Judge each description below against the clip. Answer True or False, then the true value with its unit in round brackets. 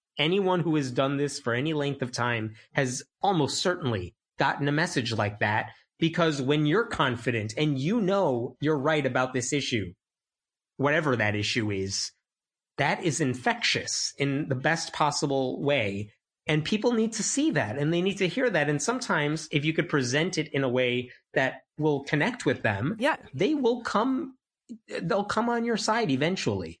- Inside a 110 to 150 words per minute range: False (175 wpm)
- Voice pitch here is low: False (145 Hz)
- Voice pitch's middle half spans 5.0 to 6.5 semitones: True (5.3 semitones)